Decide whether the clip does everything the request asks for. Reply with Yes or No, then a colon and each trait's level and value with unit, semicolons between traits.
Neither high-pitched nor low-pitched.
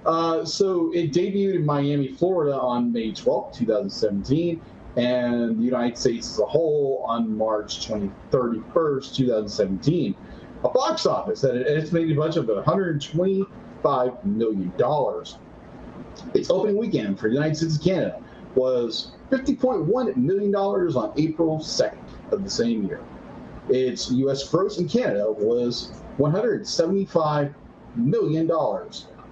Yes: medium, 155 Hz